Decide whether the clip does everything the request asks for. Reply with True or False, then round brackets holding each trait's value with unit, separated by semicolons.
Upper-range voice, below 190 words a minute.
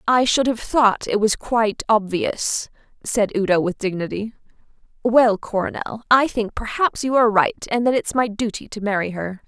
True (220 Hz; 175 wpm)